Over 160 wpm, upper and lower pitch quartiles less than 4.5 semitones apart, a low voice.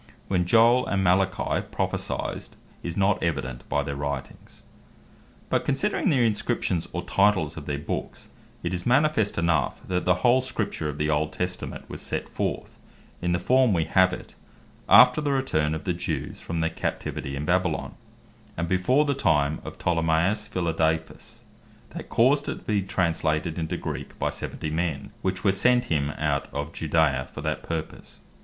No: average, 170 wpm; average, 4.8 semitones; very low, 90 Hz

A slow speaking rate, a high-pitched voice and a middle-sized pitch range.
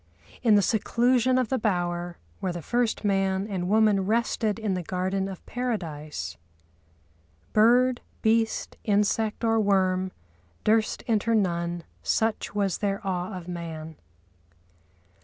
Yes: slow, 125 wpm; high, 200 Hz; average, 3.6 semitones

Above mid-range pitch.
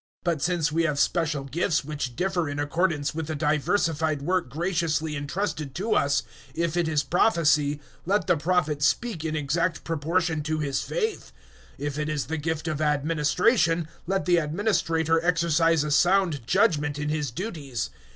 No: medium, 160 Hz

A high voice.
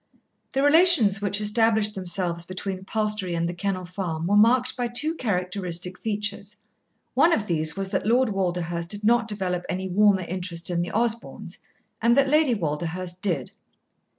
Yes: high, 195 Hz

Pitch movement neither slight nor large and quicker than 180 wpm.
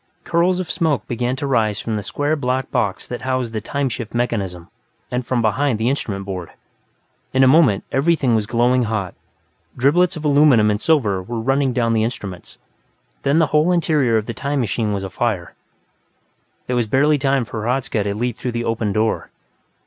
Yes: average, 4.4 semitones; average, 190 wpm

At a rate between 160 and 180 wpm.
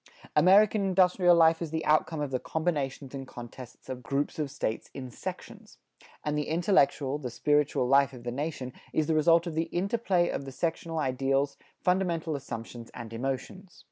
Yes: average, 175 wpm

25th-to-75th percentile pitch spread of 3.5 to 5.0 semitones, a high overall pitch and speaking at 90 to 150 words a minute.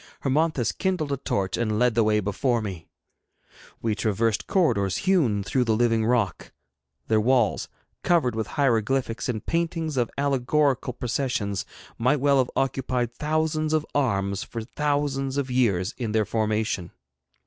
No: average, 4.6 semitones; low, 125 Hz; average, 145 wpm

